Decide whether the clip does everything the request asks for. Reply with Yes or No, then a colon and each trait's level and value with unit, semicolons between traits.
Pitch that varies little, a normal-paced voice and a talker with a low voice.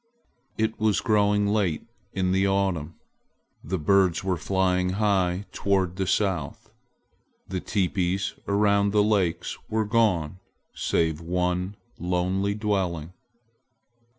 No: narrow, 2.3 semitones; slow, 110 wpm; very low, 95 Hz